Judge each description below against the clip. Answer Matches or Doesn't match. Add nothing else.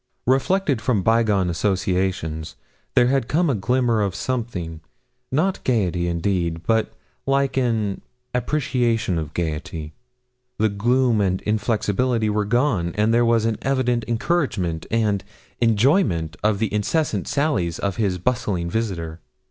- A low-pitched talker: Matches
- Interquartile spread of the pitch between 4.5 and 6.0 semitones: Matches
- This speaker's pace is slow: Matches